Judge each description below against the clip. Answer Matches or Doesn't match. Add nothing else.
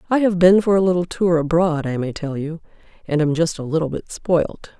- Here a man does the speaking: Doesn't match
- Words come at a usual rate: Doesn't match